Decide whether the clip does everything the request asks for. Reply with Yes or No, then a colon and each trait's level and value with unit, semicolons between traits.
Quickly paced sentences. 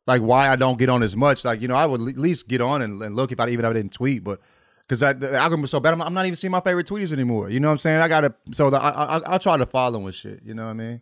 Yes: fast, 345 wpm